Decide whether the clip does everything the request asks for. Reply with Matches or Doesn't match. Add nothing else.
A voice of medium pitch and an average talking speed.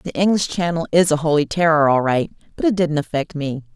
Doesn't match